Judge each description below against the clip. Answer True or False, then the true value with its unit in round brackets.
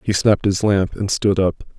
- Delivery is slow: False (235 wpm)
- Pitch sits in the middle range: False (100 Hz)